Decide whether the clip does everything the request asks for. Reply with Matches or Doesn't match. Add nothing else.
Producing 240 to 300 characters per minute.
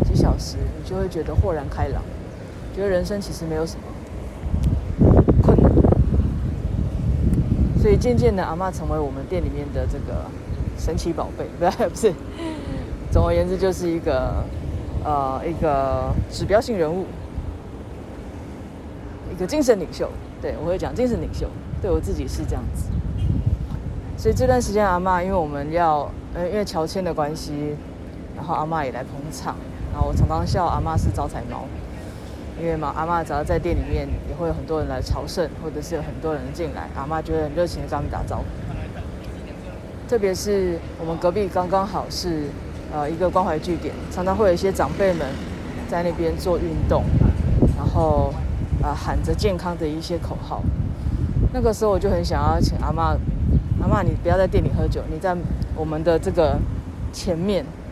Matches